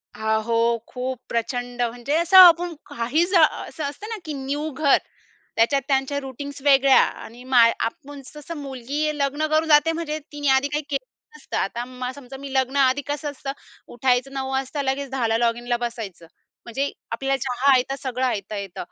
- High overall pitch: Yes, very high, 270 Hz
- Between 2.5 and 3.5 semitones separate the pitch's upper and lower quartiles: Yes, average, 2.9 semitones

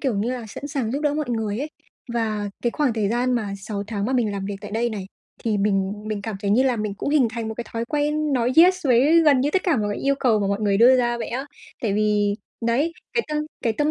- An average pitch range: Yes, average, 4.7 semitones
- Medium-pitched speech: No, high, 235 Hz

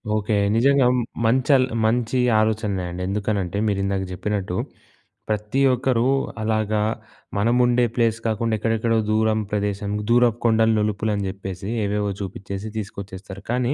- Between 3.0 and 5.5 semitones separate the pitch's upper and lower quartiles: No, narrow, 2.5 semitones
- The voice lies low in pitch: Yes, low, 110 Hz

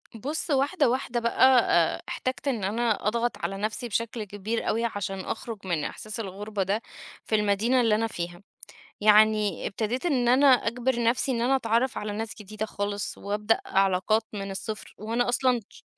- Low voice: No, high, 220 Hz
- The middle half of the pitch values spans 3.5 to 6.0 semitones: No, average, 2.9 semitones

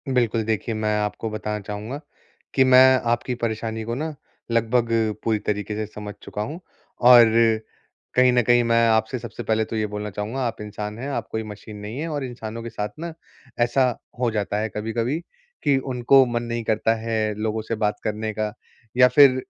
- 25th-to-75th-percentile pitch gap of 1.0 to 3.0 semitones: Yes, narrow, 2.5 semitones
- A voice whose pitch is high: No, low, 115 Hz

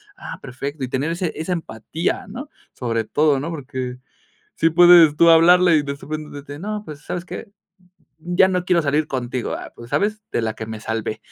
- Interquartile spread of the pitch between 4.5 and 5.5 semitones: Yes, average, 5.2 semitones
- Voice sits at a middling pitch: Yes, medium, 155 Hz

